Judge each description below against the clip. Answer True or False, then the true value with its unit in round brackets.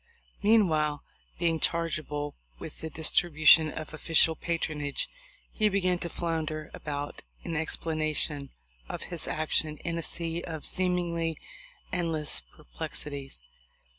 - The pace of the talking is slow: True (120 wpm)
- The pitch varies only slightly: True (1.9 semitones)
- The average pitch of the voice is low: False (160 Hz)